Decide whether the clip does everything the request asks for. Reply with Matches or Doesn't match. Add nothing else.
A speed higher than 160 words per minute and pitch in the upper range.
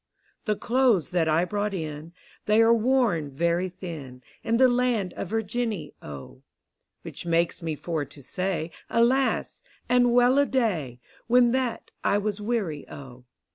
Doesn't match